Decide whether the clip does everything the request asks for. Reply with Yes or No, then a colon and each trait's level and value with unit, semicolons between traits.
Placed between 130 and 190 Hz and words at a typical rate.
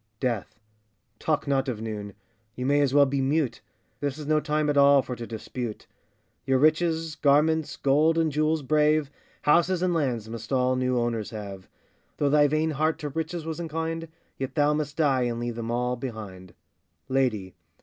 Yes: medium, 140 Hz; average, 180 wpm